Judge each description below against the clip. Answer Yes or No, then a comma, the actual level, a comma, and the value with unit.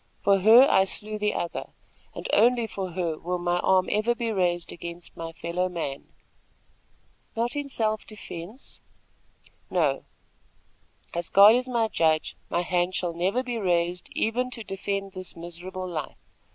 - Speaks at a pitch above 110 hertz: Yes, medium, 185 Hz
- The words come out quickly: No, average, 155 wpm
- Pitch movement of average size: Yes, average, 3.9 semitones